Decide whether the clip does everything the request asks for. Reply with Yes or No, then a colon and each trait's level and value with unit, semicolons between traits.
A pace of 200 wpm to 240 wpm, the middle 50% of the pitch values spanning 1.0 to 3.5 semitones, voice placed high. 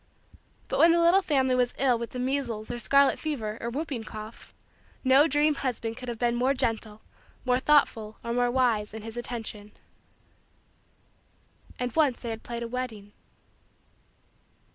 No: average, 160 wpm; average, 3.1 semitones; high, 245 Hz